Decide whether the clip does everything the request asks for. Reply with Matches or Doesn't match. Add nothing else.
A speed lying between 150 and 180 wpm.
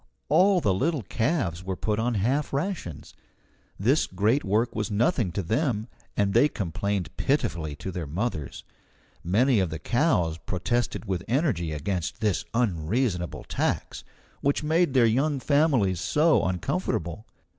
Doesn't match